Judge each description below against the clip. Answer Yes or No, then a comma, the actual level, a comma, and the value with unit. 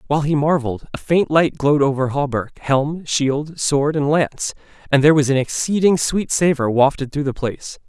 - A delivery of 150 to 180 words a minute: No, average, 190 wpm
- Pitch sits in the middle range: Yes, medium, 145 Hz